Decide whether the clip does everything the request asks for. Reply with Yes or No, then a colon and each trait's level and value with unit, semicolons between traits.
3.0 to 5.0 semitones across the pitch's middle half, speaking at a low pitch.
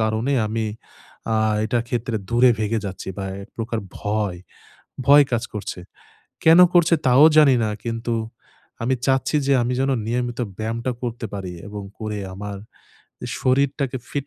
Yes: average, 3.4 semitones; low, 120 Hz